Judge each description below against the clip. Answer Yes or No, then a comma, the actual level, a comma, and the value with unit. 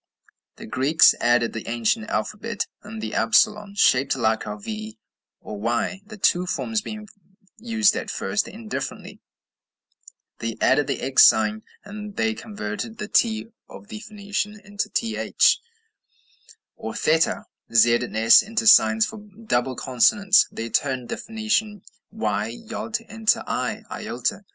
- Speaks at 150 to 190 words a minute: No, slow, 135 wpm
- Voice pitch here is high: Yes, high, 200 Hz